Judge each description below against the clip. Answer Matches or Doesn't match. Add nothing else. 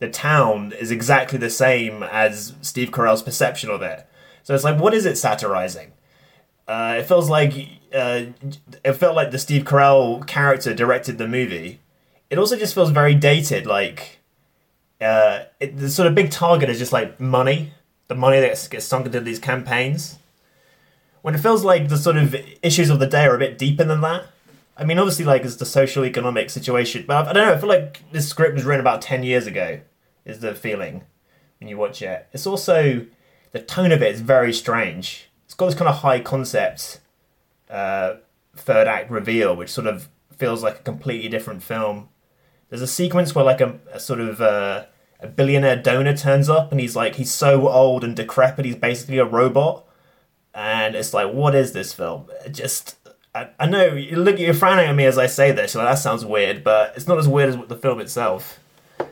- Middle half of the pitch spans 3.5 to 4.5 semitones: Matches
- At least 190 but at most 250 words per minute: Matches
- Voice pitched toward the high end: Doesn't match